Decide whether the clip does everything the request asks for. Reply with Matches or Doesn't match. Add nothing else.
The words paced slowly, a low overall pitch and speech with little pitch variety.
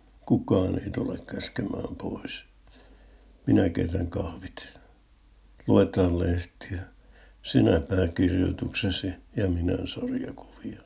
Matches